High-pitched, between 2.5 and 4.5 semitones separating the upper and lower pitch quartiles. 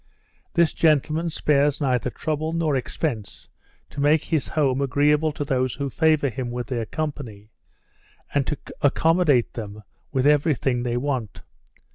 No: medium, 140 Hz; average, 3.6 semitones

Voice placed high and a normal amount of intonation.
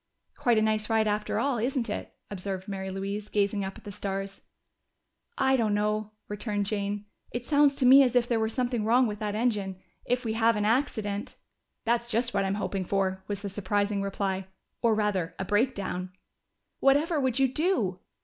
Yes: high, 210 Hz; average, 3.2 semitones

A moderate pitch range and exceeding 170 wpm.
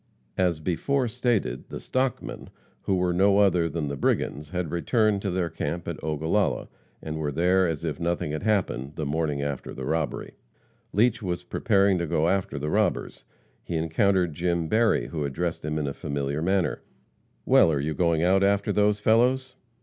Yes: average, 4.5 semitones; average, 180 wpm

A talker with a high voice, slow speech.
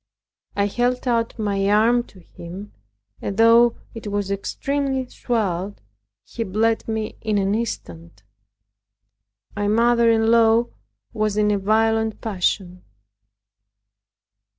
Yes: high, 215 Hz; slow, 115 wpm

